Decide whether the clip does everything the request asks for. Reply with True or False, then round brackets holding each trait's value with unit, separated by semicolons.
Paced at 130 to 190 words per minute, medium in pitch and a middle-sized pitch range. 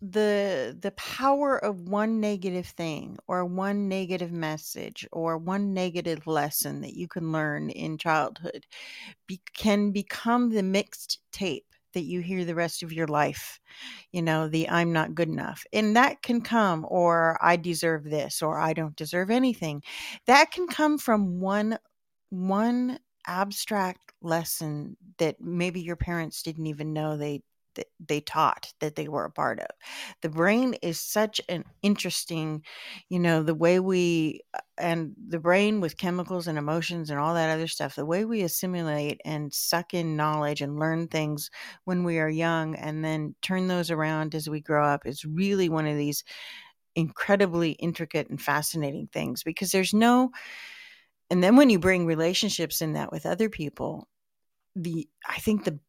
True (165 wpm; 170 Hz; 4.1 semitones)